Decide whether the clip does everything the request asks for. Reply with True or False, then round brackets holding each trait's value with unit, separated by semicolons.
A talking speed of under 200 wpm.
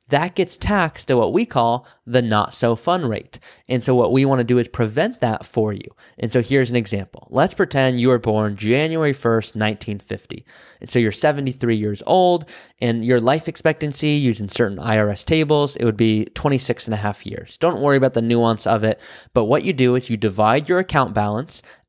False (205 wpm)